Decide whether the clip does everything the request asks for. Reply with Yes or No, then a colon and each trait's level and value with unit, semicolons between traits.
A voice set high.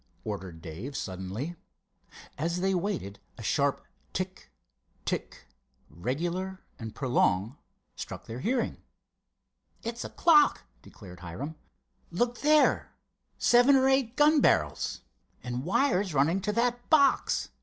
No: medium, 175 Hz